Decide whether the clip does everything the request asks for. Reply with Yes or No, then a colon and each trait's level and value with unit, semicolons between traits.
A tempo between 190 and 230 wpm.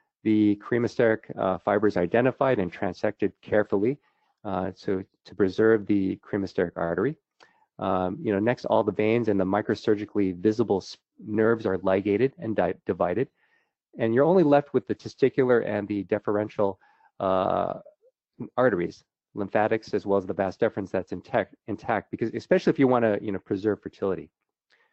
No: average, 155 wpm